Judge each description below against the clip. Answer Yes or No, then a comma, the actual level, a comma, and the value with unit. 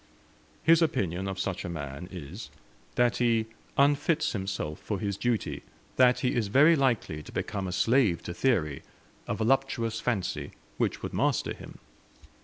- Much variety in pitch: Yes, wide, 5.9 semitones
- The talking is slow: No, average, 155 wpm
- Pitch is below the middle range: Yes, low, 110 Hz